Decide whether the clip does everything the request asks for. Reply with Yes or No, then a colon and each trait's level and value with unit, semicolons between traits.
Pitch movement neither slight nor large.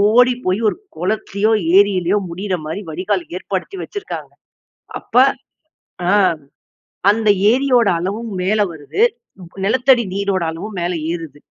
Yes: average, 3.7 semitones